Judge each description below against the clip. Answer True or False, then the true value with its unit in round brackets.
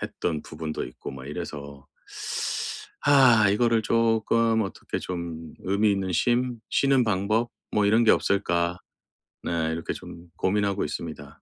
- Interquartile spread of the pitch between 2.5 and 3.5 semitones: False (5.3 semitones)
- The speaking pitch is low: True (100 Hz)